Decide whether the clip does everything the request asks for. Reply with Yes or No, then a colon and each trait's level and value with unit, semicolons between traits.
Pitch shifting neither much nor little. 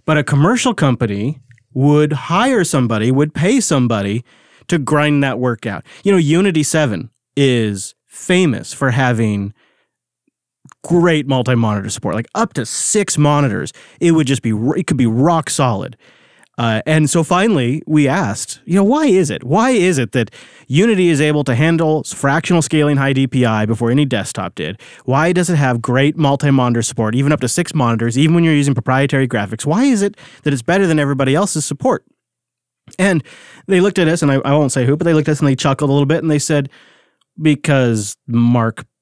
Yes: average, 4.5 semitones